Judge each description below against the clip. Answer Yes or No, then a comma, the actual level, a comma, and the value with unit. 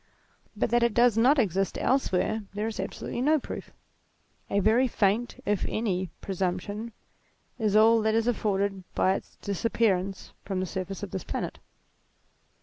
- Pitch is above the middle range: Yes, high, 210 Hz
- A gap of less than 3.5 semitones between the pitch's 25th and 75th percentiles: Yes, average, 3.1 semitones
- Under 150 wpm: No, average, 160 wpm